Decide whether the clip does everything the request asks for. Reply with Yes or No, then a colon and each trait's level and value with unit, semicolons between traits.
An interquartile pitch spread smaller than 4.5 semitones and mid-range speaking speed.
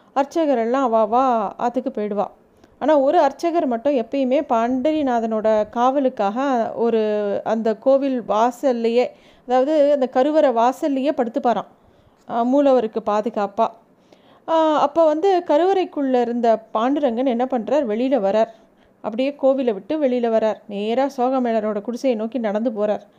Yes: average, 3.8 semitones; average, 115 wpm